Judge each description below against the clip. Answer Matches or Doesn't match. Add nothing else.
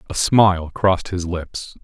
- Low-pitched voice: Matches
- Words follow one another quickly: Doesn't match